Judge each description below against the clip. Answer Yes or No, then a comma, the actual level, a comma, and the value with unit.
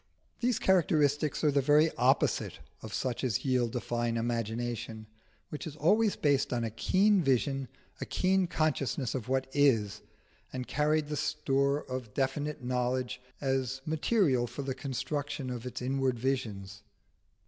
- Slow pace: No, average, 150 wpm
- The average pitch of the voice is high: No, low, 135 Hz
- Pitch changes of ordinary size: Yes, average, 3.5 semitones